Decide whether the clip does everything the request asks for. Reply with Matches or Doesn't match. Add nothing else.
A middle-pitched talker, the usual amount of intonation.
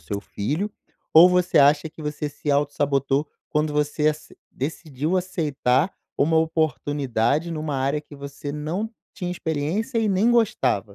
Matches